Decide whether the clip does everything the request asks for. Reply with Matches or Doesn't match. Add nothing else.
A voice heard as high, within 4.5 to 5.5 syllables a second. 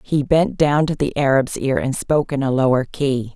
Doesn't match